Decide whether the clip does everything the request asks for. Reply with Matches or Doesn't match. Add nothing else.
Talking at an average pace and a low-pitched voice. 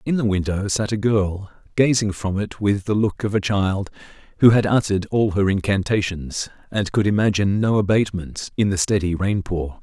Matches